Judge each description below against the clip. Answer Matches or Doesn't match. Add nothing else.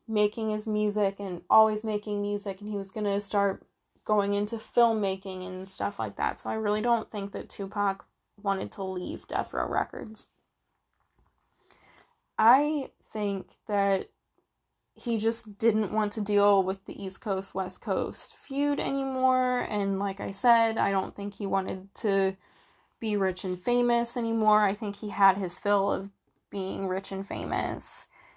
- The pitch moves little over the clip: Matches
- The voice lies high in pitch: Matches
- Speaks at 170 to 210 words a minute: Doesn't match